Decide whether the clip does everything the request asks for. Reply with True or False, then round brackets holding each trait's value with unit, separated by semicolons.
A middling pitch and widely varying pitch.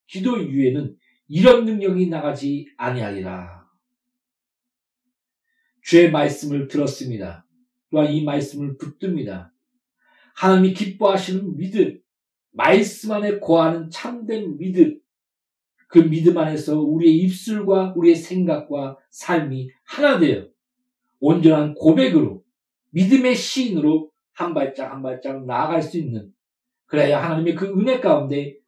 True (170 Hz; 8.7 semitones)